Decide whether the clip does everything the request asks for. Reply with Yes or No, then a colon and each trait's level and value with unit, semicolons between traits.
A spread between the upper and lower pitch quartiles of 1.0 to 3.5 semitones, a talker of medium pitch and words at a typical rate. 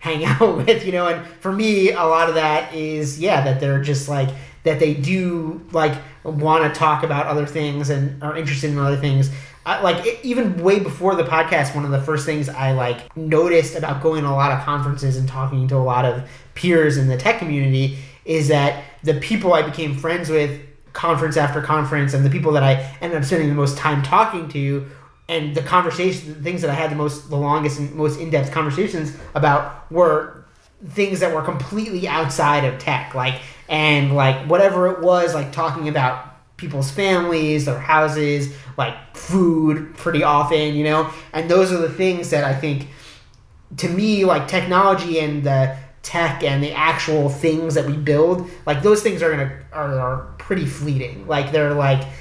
Yes: average, 2.8 semitones; medium, 155 Hz; average, 195 wpm